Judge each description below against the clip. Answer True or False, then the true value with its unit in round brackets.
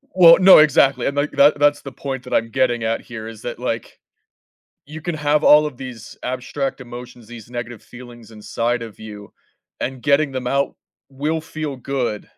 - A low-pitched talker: True (130 Hz)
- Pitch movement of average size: True (3.5 semitones)